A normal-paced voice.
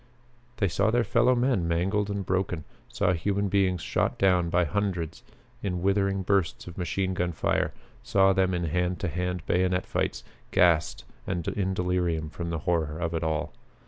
Yes: average, 175 wpm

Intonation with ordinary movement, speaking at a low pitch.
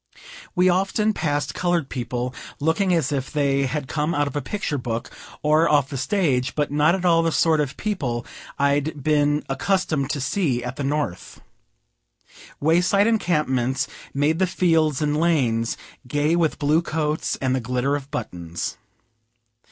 No: average, 3.7 semitones; medium, 150 Hz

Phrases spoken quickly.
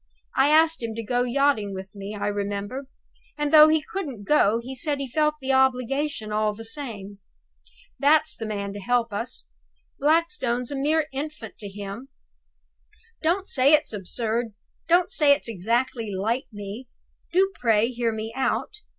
No: average, 160 wpm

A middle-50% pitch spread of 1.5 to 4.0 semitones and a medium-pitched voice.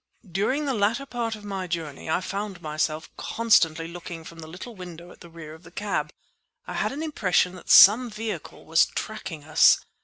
No: average, 4.8 semitones; medium, 180 Hz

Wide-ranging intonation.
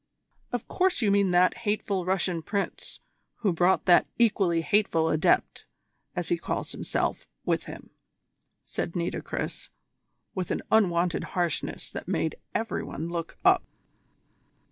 No: average, 3.3 semitones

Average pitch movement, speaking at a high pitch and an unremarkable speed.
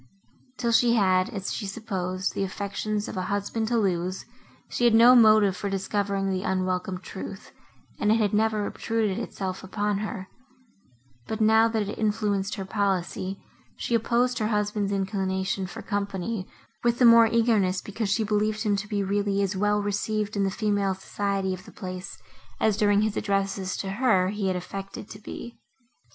No: narrow, 2.1 semitones; high, 205 Hz; average, 175 wpm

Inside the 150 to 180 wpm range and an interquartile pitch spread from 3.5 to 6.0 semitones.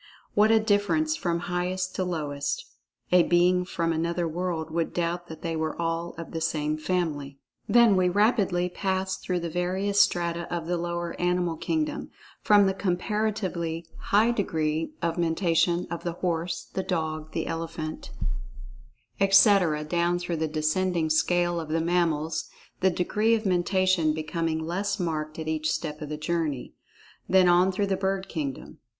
No: average, 155 wpm; narrow, 2.6 semitones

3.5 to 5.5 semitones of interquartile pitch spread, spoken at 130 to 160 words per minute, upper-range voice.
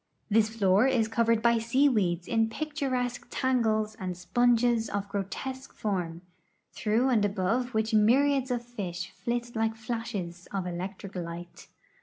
Yes: average, 3.8 semitones; average, 140 wpm; high, 225 Hz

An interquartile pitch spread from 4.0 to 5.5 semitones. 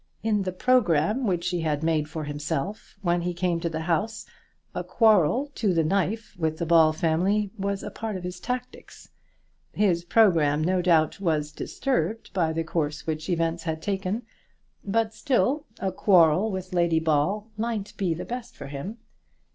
Yes: average, 4.6 semitones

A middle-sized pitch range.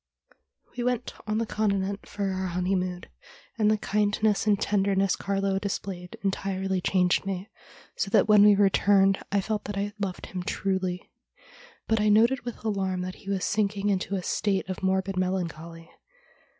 No: narrow, 1.7 semitones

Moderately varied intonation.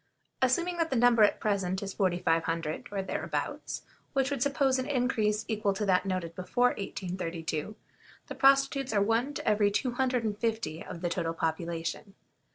No: wide, 5.7 semitones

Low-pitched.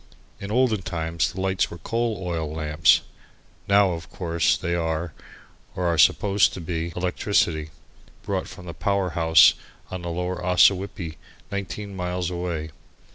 Yes: very low, 90 Hz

